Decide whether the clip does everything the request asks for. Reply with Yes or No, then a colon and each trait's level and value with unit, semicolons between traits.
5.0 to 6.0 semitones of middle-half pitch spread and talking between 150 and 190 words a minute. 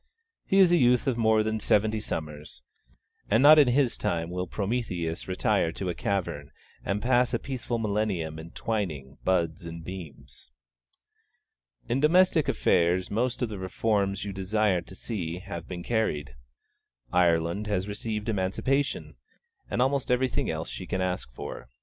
Yes: wide, 5.4 semitones; average, 155 wpm